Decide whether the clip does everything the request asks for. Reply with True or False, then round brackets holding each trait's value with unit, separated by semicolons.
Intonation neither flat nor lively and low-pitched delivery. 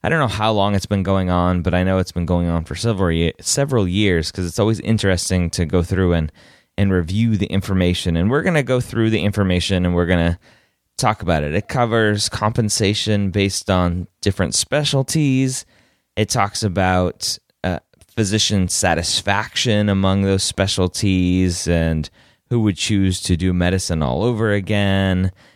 True (3.1 semitones; 95 Hz)